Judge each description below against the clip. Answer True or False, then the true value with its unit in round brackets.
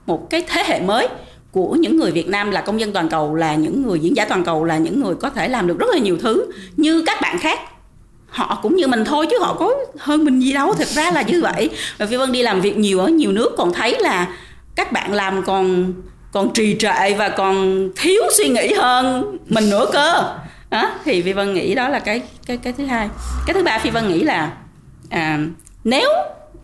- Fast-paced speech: False (235 wpm)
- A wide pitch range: True (7.2 semitones)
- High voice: True (215 Hz)